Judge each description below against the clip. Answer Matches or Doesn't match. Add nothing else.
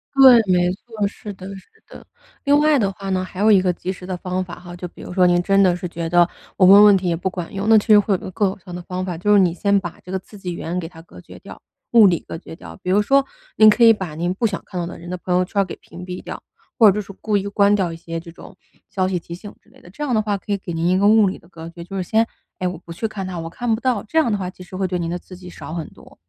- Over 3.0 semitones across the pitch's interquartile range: Doesn't match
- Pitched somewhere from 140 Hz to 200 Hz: Matches